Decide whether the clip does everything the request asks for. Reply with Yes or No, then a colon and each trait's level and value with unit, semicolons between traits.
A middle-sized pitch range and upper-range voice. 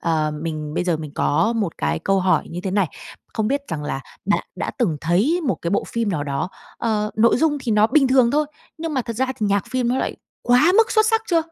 No: wide, 7.5 semitones; high, 220 Hz